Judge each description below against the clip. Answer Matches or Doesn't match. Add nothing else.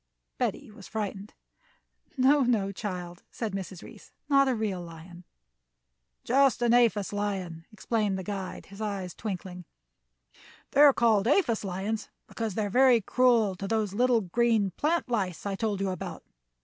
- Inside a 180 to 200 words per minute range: Doesn't match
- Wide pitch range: Doesn't match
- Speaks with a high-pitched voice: Matches